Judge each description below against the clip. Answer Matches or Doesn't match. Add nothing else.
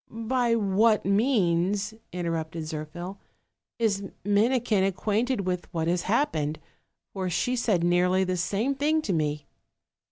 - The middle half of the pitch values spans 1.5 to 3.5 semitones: Doesn't match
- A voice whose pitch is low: Doesn't match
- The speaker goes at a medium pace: Doesn't match